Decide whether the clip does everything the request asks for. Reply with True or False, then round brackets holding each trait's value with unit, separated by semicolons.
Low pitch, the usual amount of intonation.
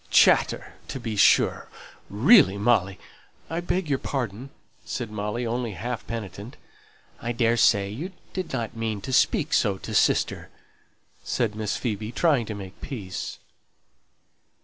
True (115 Hz; 3.6 semitones)